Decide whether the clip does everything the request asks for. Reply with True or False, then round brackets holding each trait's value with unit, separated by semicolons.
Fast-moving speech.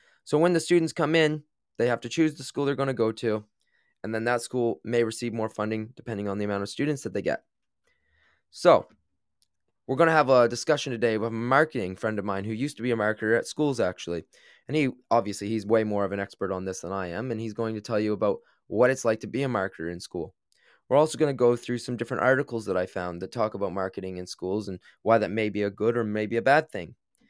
True (255 wpm)